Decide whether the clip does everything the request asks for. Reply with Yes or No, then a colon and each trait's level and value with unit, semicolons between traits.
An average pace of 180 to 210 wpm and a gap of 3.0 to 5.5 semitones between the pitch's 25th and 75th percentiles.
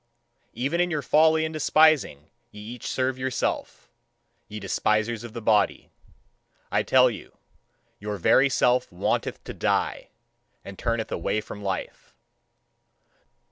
No: slow, 135 wpm; average, 4.9 semitones